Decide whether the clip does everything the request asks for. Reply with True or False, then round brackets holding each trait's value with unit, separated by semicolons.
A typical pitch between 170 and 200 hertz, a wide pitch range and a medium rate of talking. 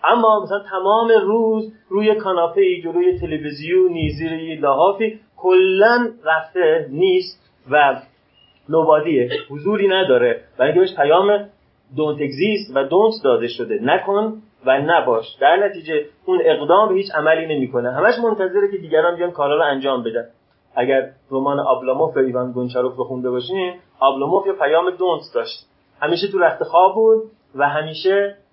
True (190 Hz; 6.6 semitones; 145 wpm)